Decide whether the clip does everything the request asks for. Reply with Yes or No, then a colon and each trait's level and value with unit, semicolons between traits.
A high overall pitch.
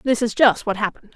Yes: high, 220 Hz